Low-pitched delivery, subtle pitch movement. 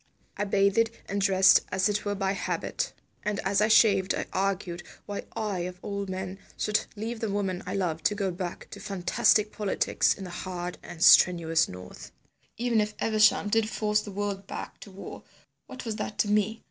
No: high, 200 Hz; narrow, 2.0 semitones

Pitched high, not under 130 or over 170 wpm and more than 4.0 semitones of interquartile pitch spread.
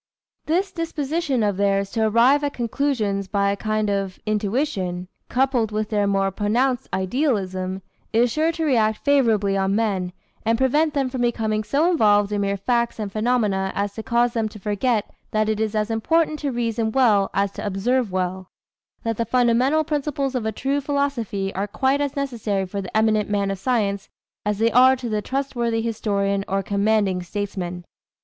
No: high, 220 Hz; average, 180 wpm; average, 4.4 semitones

